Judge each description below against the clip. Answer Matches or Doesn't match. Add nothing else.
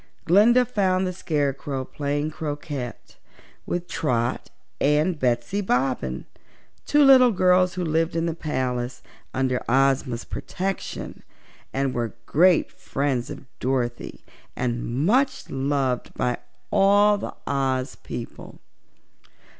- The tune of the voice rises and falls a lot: Matches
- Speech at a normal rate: Doesn't match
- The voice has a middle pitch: Matches